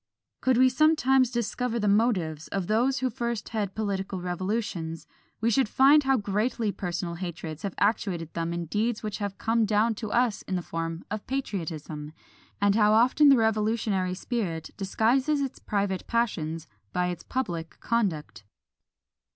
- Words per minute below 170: Yes, average, 155 wpm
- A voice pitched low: No, high, 210 Hz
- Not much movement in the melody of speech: No, average, 4.9 semitones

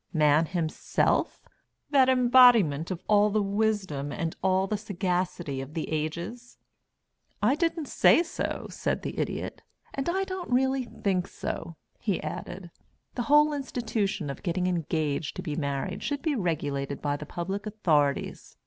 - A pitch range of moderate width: No, wide, 7.4 semitones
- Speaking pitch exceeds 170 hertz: Yes, high, 190 Hz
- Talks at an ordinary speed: Yes, average, 150 wpm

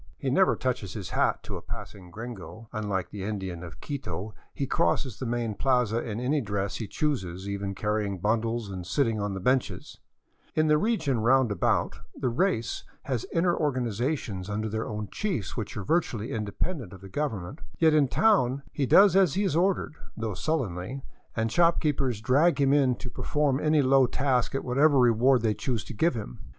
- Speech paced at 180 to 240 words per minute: Yes, average, 185 wpm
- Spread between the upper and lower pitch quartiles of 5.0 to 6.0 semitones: Yes, wide, 5.5 semitones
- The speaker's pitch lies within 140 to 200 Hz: No, low, 120 Hz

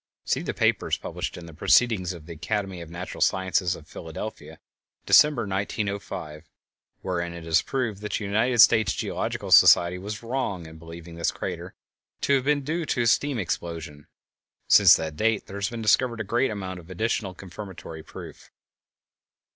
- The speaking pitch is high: No, very low, 95 Hz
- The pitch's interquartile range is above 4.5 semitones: Yes, average, 4.9 semitones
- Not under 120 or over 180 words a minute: Yes, average, 170 wpm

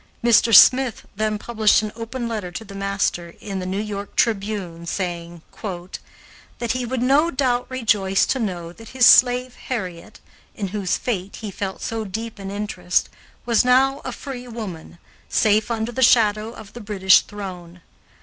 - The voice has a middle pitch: No, high, 215 Hz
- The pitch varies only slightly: No, average, 3.8 semitones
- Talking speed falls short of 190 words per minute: Yes, average, 165 wpm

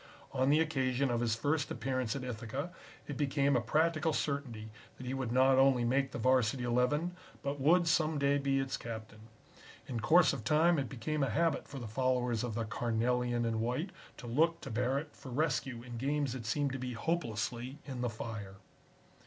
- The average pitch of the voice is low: Yes, low, 130 Hz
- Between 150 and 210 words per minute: Yes, average, 195 wpm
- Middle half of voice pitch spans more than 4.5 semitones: No, average, 3.3 semitones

